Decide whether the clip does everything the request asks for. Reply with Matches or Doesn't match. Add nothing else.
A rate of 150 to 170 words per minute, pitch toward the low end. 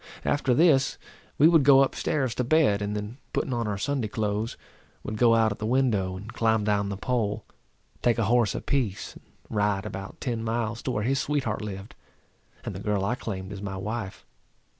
Doesn't match